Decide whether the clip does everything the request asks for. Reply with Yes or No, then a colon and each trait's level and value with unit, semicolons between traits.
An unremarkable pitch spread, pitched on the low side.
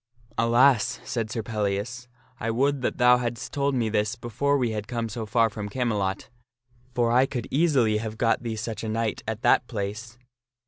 No: narrow, 2.3 semitones; low, 115 Hz